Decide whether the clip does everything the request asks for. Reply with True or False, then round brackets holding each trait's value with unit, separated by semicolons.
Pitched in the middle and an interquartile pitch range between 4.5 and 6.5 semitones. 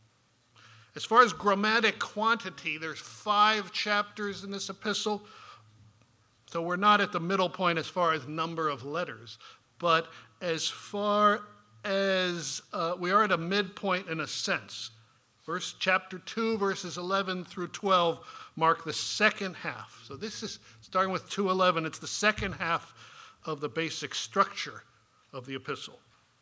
True (180 Hz; 4.8 semitones)